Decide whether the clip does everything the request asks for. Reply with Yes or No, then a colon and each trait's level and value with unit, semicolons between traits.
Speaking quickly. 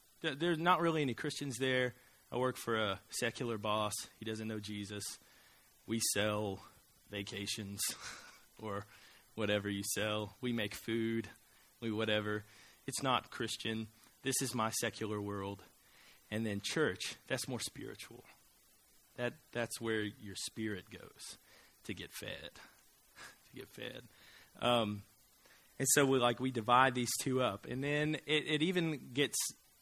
No: average, 140 wpm